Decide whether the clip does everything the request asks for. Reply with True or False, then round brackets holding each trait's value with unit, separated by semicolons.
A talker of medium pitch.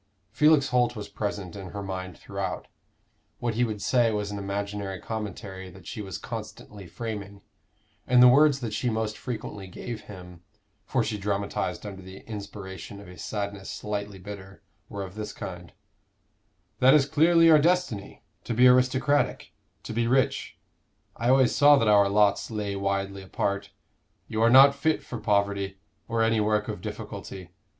False (105 Hz)